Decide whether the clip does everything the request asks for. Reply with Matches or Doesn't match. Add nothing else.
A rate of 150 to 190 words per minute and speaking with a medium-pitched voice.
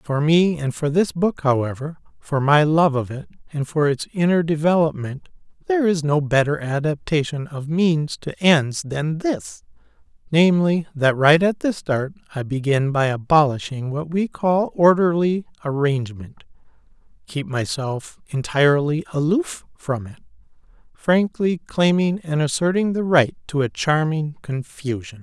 Doesn't match